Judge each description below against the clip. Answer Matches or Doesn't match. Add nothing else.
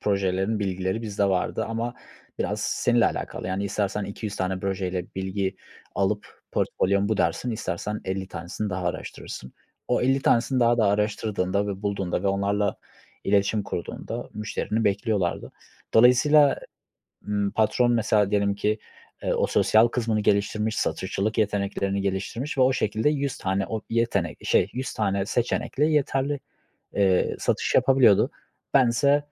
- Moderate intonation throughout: Matches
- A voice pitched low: Matches